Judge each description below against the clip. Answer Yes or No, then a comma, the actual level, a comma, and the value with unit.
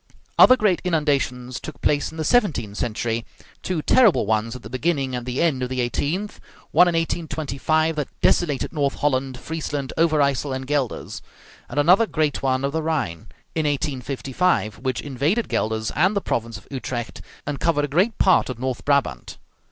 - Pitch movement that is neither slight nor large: Yes, average, 4.1 semitones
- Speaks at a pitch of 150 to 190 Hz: No, medium, 140 Hz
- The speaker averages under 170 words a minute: No, average, 175 wpm